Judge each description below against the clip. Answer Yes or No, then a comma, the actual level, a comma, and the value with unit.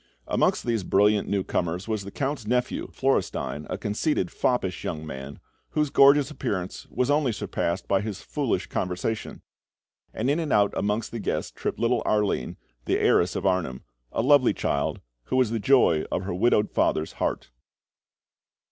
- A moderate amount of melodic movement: No, wide, 5.7 semitones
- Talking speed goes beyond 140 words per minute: Yes, average, 160 wpm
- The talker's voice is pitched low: Yes, low, 105 Hz